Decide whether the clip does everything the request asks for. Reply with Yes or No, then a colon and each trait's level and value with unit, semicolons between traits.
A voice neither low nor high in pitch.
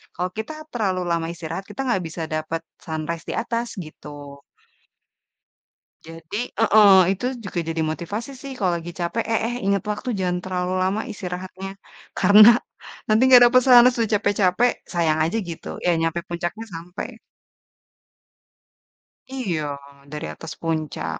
Yes: medium, 180 Hz